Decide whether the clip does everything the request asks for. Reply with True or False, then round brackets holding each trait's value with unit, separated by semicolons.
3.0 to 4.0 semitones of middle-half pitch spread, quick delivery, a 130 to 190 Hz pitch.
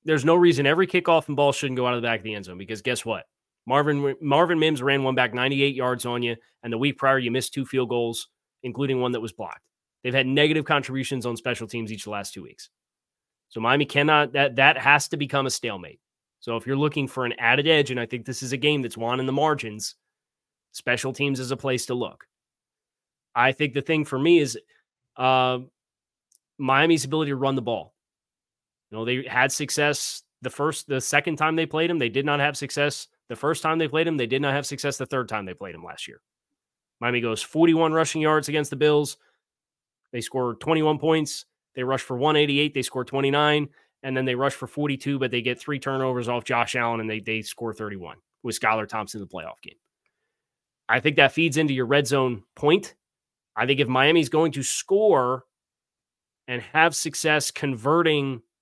True (3.4 semitones; 215 wpm; 135 Hz)